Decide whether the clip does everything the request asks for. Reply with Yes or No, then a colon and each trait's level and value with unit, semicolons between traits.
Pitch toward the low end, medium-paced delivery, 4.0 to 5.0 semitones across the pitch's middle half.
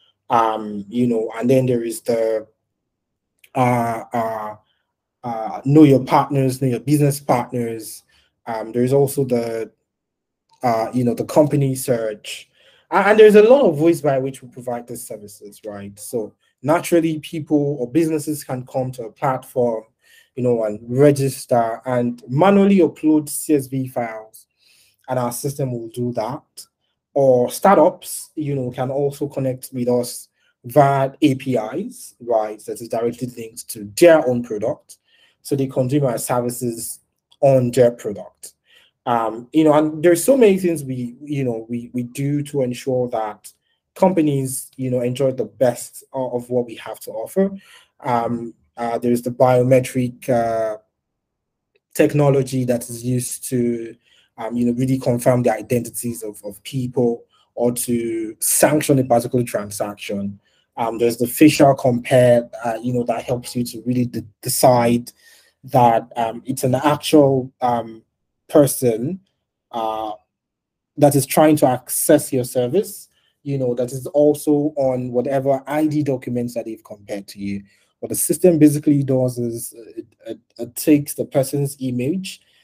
No: low, 125 Hz; average, 155 wpm; average, 3.1 semitones